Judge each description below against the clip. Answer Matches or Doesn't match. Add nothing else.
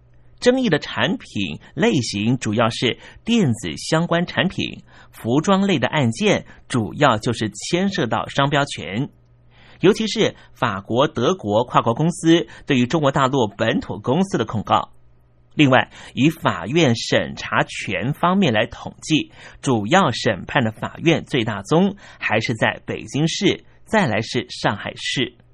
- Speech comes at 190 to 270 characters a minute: Matches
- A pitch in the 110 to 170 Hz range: Matches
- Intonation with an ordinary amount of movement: Doesn't match